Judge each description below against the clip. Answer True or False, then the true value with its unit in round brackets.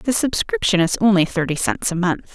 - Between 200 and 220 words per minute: True (205 wpm)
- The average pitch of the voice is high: True (200 Hz)